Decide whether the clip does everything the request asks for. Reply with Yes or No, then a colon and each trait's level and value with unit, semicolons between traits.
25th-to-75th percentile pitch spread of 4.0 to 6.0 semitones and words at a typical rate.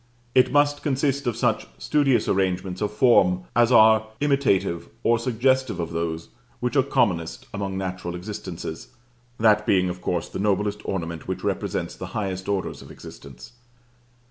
Yes: average, 5.2 semitones; average, 150 wpm